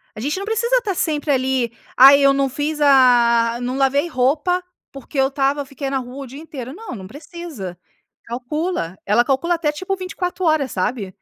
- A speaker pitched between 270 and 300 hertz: Yes, very high, 275 Hz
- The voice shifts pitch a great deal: No, average, 4.2 semitones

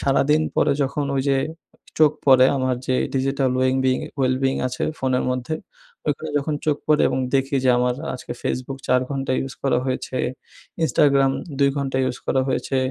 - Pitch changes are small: Yes, narrow, 1.3 semitones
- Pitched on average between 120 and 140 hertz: Yes, low, 135 Hz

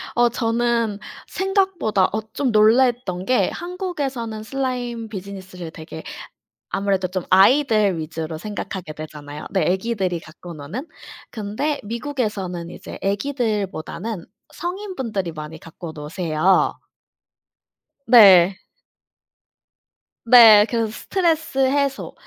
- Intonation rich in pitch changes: Yes, wide, 5.7 semitones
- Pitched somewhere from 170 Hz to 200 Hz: No, high, 215 Hz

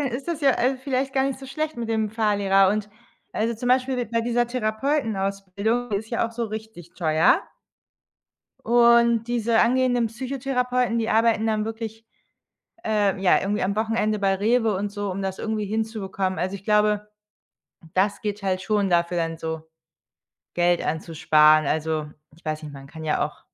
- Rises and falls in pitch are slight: No, average, 3.7 semitones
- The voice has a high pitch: Yes, high, 215 Hz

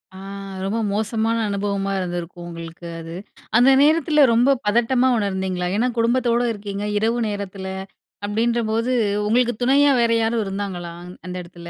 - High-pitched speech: Yes, high, 210 Hz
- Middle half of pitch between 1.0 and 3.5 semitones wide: No, average, 3.9 semitones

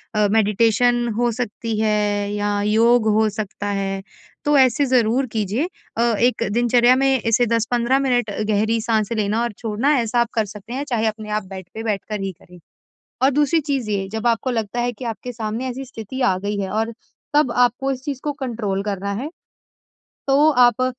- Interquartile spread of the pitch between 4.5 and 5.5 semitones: No, average, 2.9 semitones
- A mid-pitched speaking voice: No, high, 230 Hz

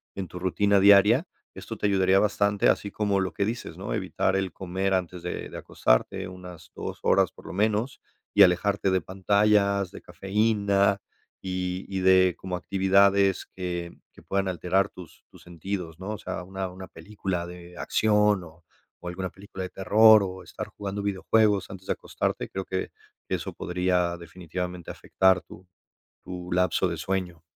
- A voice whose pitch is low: Yes, very low, 95 Hz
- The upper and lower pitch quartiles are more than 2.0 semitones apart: No, narrow, 1.7 semitones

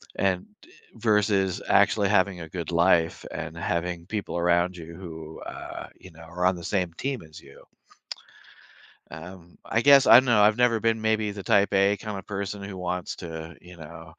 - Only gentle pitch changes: No, average, 3.4 semitones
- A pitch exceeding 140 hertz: No, very low, 95 Hz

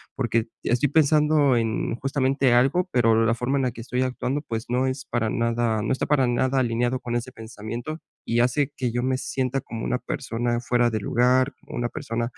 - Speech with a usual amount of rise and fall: No, narrow, 2.1 semitones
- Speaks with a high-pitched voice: No, low, 125 Hz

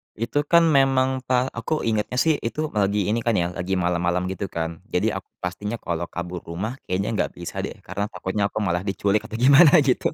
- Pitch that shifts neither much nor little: No, wide, 5.9 semitones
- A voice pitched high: No, low, 105 Hz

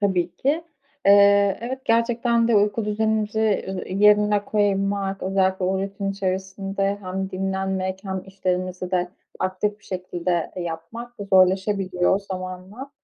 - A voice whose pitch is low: No, high, 195 Hz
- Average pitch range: No, narrow, 2.0 semitones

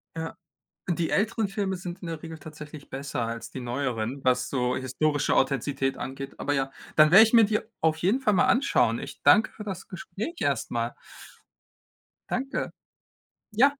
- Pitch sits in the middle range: Yes, medium, 160 Hz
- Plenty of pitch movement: Yes, wide, 7.1 semitones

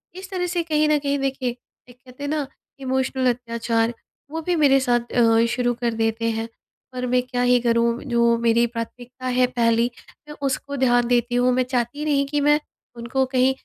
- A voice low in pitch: No, very high, 250 Hz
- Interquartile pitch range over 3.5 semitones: No, narrow, 2.6 semitones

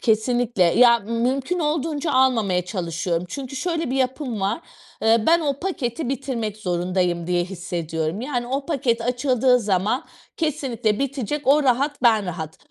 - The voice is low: No, high, 240 Hz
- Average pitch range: No, wide, 6.0 semitones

